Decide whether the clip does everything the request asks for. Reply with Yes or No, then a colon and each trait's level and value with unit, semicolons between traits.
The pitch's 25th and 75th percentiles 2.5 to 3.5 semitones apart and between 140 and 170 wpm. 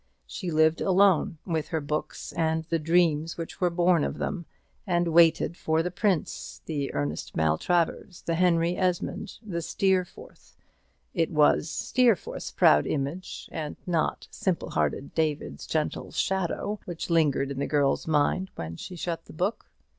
Yes: average, 2.8 semitones; average, 150 wpm